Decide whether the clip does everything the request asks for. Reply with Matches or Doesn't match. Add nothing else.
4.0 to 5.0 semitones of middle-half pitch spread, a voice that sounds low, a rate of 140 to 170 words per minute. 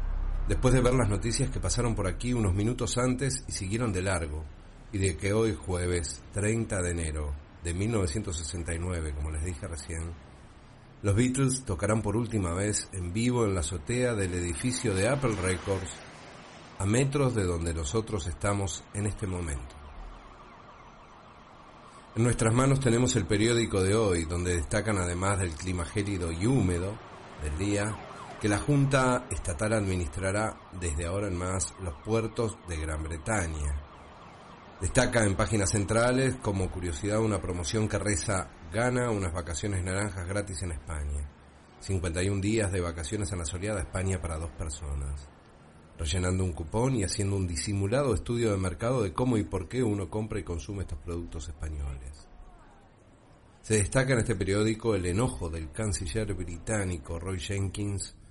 Matches